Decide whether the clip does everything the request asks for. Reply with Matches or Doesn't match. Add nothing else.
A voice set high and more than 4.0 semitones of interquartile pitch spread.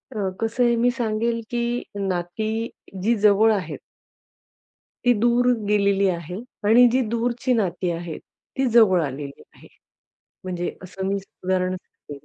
Matches